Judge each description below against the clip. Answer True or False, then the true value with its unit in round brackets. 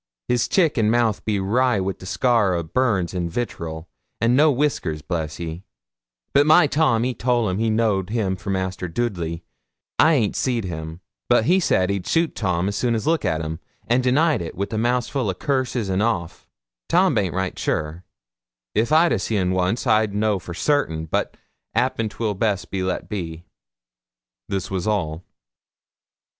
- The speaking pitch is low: True (105 Hz)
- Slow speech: False (170 wpm)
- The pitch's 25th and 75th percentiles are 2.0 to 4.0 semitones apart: False (5.2 semitones)